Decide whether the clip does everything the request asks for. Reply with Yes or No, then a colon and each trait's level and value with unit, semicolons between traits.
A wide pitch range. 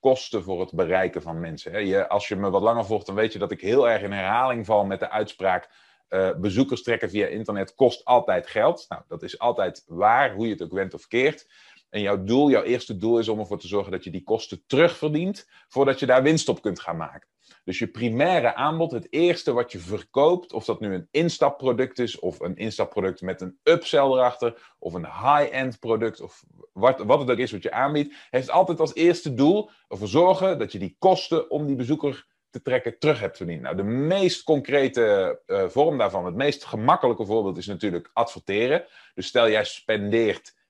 Yes: wide, 6.4 semitones